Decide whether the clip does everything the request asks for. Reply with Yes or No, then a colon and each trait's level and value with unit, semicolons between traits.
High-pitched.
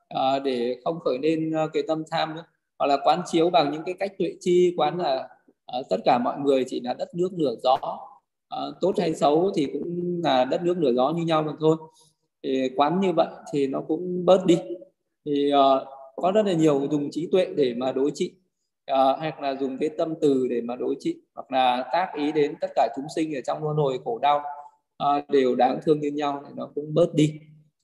No: medium, 155 Hz